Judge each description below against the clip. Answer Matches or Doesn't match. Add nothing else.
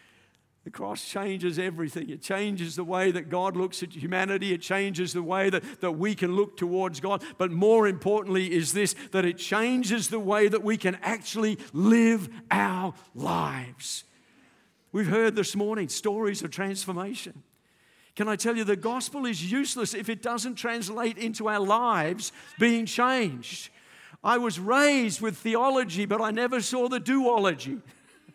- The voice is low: Doesn't match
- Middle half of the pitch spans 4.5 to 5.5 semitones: Doesn't match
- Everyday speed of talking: Matches